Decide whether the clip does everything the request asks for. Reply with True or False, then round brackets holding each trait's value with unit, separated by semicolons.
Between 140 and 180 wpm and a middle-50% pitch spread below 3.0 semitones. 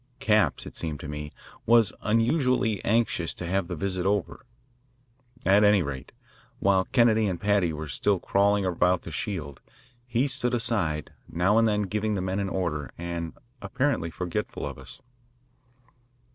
False (155 wpm; 4.2 semitones)